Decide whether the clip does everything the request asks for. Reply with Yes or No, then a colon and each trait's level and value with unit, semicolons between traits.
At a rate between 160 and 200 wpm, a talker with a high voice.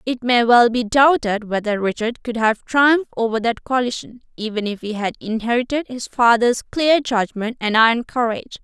Yes: average, 175 wpm; high, 235 Hz